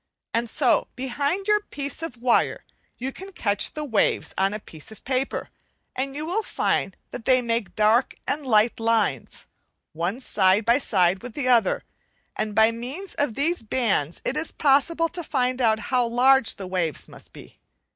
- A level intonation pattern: No, average, 4.5 semitones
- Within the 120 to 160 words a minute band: No, average, 175 wpm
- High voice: Yes, high, 245 Hz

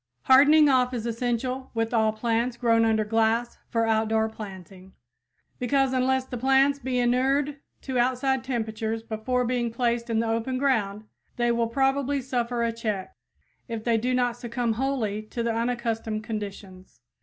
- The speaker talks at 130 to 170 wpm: Yes, average, 155 wpm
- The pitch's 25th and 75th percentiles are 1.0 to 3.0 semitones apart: Yes, narrow, 2.4 semitones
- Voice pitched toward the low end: No, high, 235 Hz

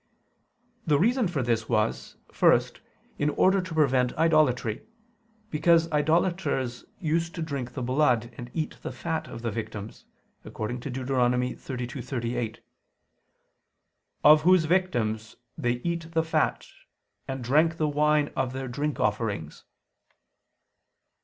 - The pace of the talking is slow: Yes, slow, 125 wpm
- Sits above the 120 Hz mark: Yes, low, 135 Hz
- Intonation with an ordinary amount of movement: Yes, average, 5.0 semitones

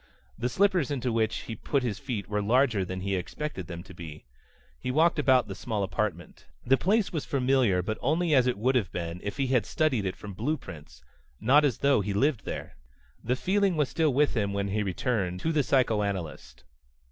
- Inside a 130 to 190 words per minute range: No, fast, 205 wpm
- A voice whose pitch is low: Yes, low, 120 Hz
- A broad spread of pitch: Yes, wide, 5.9 semitones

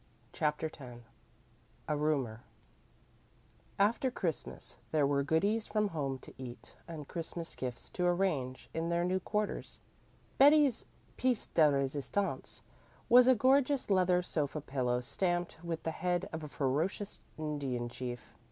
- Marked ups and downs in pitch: Yes, wide, 5.8 semitones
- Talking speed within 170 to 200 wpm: No, slow, 135 wpm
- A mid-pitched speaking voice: Yes, medium, 160 Hz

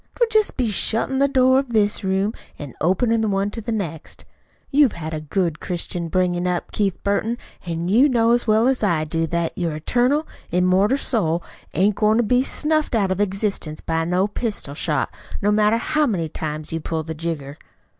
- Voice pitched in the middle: No, high, 195 Hz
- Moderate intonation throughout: No, wide, 5.8 semitones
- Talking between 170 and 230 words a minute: Yes, average, 195 wpm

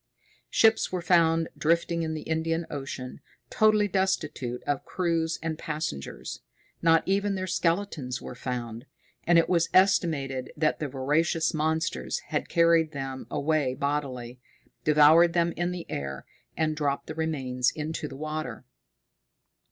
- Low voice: No, medium, 160 Hz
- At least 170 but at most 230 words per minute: No, slow, 135 wpm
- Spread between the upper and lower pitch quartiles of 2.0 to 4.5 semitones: Yes, average, 3.4 semitones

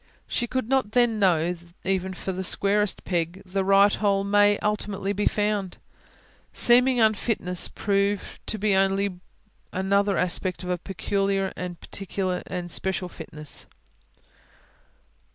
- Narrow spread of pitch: Yes, narrow, 2.2 semitones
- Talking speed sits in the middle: No, slow, 125 wpm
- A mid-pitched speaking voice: No, high, 195 Hz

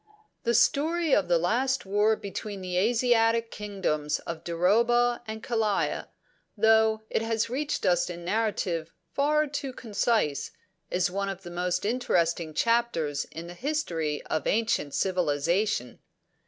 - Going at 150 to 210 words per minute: No, average, 140 wpm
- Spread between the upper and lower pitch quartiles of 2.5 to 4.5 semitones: No, average, 5.1 semitones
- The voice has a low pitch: No, high, 205 Hz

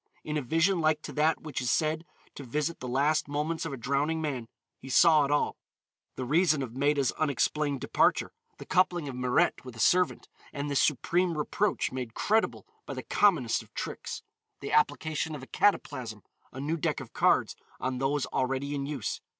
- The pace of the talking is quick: No, average, 190 wpm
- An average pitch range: Yes, average, 3.2 semitones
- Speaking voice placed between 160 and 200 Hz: No, medium, 145 Hz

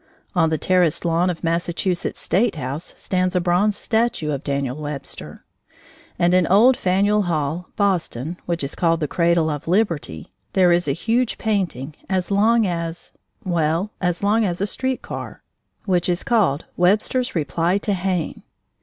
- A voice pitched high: No, medium, 175 Hz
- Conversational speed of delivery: Yes, average, 160 wpm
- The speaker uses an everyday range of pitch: Yes, average, 3.6 semitones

